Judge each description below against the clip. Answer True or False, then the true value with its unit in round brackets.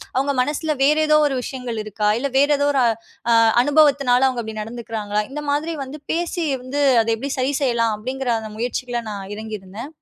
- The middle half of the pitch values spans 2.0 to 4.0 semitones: False (4.4 semitones)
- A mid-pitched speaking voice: False (255 Hz)